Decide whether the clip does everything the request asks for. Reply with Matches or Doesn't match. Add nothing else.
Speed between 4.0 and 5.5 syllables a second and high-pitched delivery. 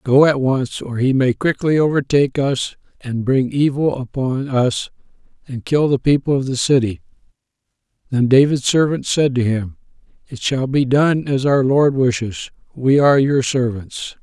Doesn't match